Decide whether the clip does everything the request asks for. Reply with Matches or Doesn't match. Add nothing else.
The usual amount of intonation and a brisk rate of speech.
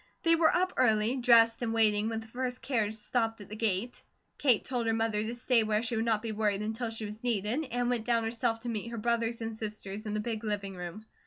Doesn't match